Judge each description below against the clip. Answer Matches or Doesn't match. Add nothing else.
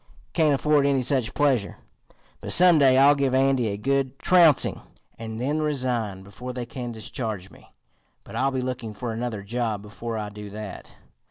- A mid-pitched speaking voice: Doesn't match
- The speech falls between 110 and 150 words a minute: Doesn't match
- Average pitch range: Matches